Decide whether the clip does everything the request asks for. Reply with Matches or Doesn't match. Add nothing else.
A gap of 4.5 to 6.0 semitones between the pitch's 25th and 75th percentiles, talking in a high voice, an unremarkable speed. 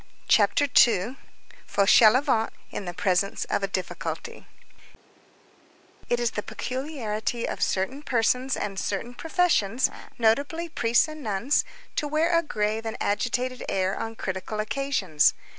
Doesn't match